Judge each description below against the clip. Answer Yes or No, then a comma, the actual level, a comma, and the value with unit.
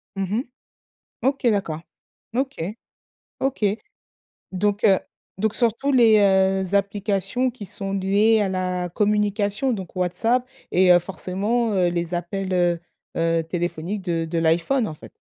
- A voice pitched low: No, high, 195 Hz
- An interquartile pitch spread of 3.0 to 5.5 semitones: Yes, average, 3.4 semitones